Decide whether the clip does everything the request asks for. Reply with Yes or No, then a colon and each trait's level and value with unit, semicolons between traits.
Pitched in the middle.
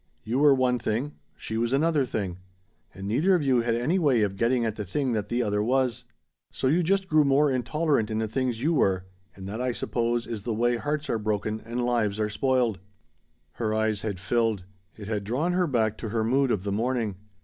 No: low, 120 Hz